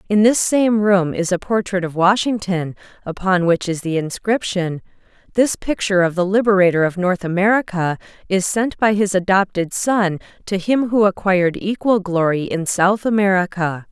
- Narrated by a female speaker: Yes, female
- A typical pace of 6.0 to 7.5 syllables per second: No, 4.9 syllables/s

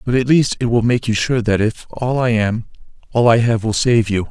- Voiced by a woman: No, male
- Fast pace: Yes, fast, 265 wpm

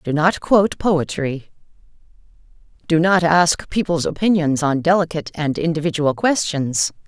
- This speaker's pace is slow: Yes, slow, 120 wpm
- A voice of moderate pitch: Yes, medium, 165 Hz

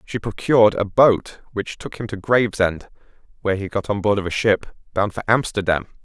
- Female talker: No, male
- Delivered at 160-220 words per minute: Yes, average, 200 wpm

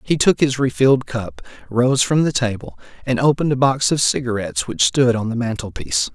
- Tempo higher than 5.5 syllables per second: Yes, 5.7 syllables/s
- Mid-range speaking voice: No, low, 125 Hz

